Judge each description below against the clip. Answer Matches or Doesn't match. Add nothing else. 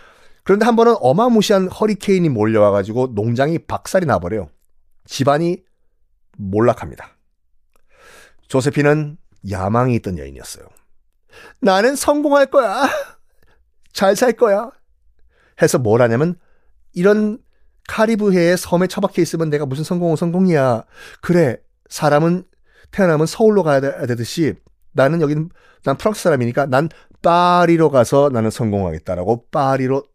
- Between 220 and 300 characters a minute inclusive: Matches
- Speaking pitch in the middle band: Matches